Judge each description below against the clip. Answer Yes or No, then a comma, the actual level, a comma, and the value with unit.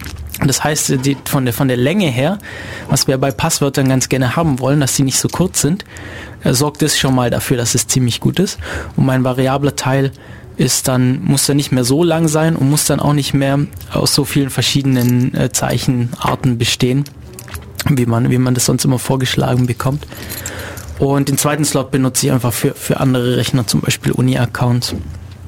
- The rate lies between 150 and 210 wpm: Yes, average, 185 wpm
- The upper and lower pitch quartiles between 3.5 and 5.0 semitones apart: No, narrow, 2.6 semitones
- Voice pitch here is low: Yes, low, 130 Hz